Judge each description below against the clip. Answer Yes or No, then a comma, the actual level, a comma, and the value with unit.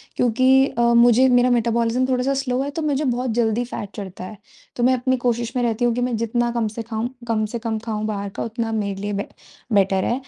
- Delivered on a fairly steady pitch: Yes, narrow, 2.3 semitones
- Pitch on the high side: Yes, high, 235 Hz